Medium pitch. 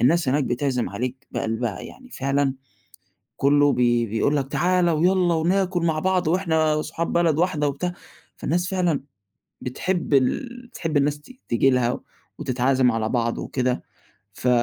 Yes: medium, 145 Hz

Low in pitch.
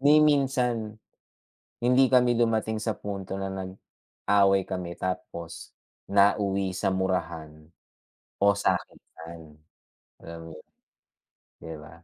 Yes: very low, 95 Hz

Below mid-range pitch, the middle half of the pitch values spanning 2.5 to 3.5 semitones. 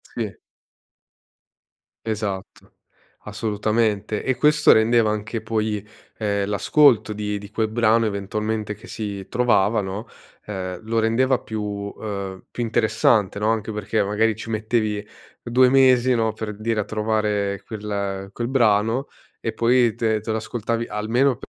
No: low, 110 Hz; narrow, 1.8 semitones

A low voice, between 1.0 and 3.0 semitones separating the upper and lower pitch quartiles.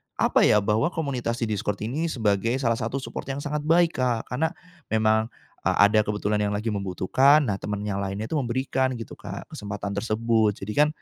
No: low, 115 Hz; average, 4.1 semitones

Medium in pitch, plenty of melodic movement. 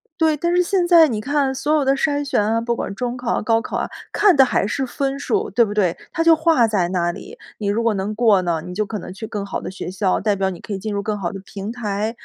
No: high, 225 Hz; wide, 6.0 semitones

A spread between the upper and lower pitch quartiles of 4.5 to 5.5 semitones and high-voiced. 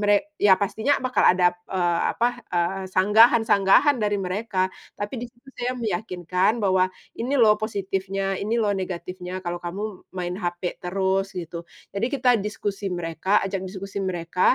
No: average, 2.7 semitones; high, 195 Hz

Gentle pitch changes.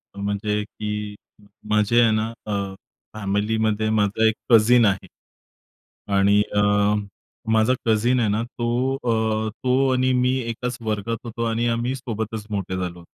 Yes: narrow, 2.2 semitones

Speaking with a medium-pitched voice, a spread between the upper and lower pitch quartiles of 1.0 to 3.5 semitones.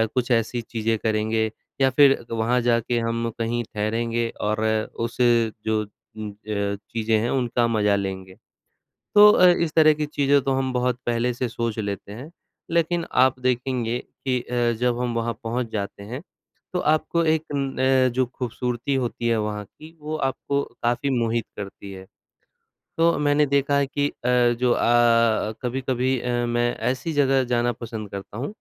No: low, 120 Hz; average, 3.0 semitones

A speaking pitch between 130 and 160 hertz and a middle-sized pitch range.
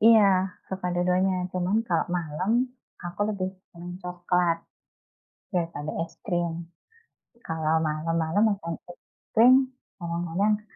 No: medium, 180 Hz; average, 3.0 semitones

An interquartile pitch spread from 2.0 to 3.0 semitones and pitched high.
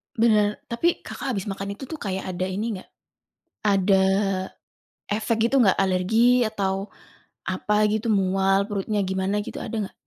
Yes: narrow, 2.5 semitones; high, 205 Hz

